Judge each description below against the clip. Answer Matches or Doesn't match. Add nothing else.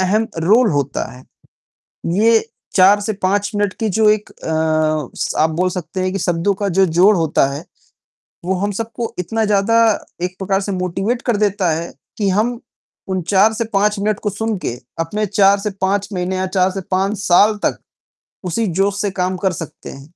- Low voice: Doesn't match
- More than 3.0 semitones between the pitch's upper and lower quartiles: Doesn't match